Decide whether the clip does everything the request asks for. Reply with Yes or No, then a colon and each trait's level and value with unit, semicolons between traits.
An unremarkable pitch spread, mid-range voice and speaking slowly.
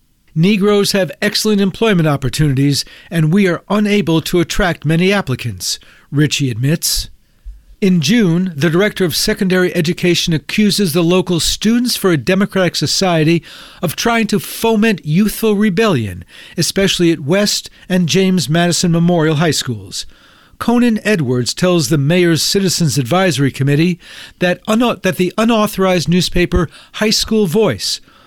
Yes: average, 4.2 semitones; medium, 180 Hz; slow, 130 wpm